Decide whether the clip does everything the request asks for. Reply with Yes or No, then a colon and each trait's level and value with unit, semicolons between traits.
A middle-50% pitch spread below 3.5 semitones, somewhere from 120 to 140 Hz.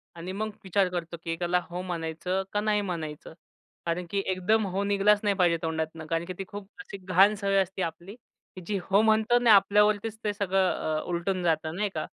No: average, 3.1 semitones; high, 190 Hz